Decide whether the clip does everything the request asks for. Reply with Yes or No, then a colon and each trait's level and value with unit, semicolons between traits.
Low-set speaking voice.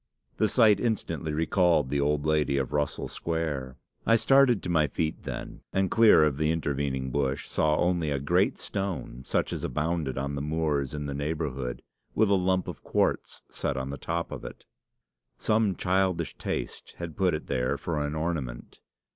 Yes: very low, 80 Hz